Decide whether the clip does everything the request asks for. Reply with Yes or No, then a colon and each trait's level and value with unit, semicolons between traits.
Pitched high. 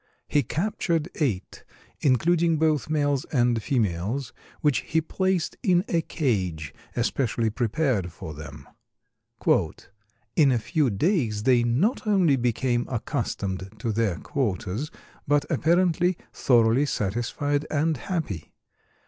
No: low, 130 Hz